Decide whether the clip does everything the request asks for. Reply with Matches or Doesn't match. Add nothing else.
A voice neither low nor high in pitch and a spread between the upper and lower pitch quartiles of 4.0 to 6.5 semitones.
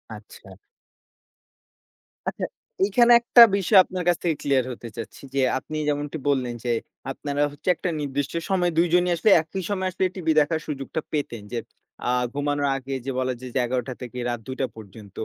Matches